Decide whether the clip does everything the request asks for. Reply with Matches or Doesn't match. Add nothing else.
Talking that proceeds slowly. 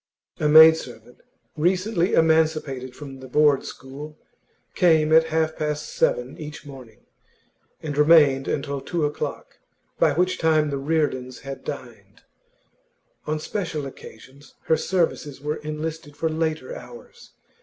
Matches